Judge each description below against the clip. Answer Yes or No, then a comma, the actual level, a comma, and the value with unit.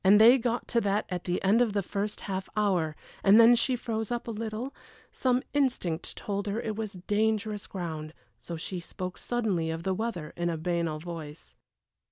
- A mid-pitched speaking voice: No, high, 200 Hz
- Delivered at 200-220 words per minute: No, average, 190 wpm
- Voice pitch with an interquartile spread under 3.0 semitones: No, average, 4.5 semitones